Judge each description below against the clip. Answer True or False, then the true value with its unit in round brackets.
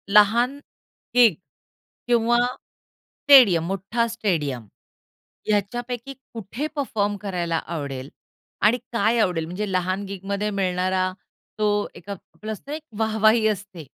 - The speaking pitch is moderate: False (205 Hz)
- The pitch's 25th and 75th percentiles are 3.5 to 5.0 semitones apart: True (3.9 semitones)